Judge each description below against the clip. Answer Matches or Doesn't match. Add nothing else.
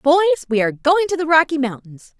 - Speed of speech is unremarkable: Doesn't match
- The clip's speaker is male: Doesn't match